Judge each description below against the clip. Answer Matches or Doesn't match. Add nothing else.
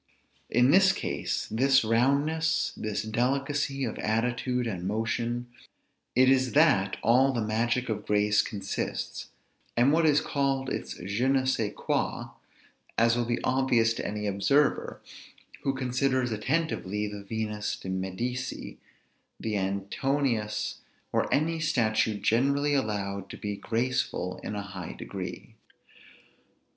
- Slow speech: Matches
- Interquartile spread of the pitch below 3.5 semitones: Doesn't match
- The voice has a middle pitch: Doesn't match